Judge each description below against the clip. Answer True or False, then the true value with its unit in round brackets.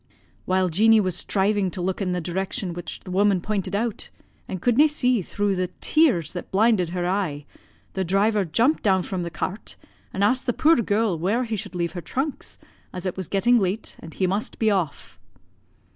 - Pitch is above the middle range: True (195 Hz)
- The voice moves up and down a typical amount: True (3.4 semitones)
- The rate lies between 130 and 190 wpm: False (200 wpm)